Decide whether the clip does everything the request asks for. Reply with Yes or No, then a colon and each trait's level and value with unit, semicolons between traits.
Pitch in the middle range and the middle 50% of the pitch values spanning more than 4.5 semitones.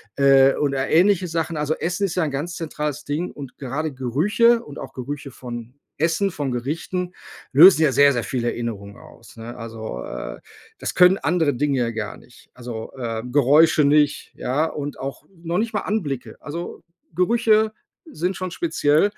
Yes: medium, 145 Hz; average, 5.0 semitones